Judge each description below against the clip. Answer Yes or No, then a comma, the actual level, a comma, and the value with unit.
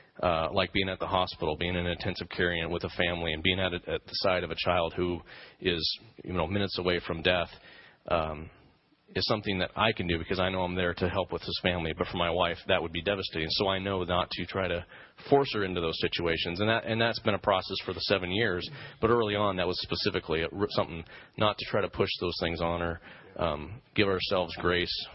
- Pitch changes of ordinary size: No, narrow, 2.2 semitones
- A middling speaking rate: No, fast, 240 wpm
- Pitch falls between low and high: No, very low, 90 Hz